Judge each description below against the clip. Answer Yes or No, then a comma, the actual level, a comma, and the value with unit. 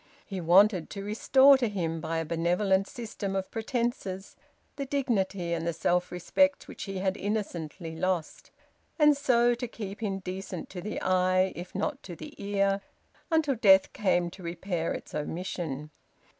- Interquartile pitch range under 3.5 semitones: No, average, 4.0 semitones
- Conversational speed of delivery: Yes, average, 160 wpm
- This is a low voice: No, high, 190 Hz